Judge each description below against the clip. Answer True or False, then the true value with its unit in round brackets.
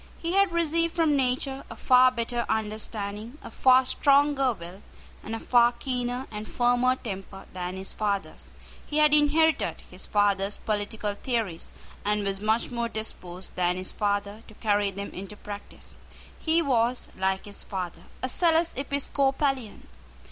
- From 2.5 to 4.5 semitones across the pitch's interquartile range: False (5.0 semitones)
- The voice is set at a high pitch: True (230 Hz)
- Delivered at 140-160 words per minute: True (150 wpm)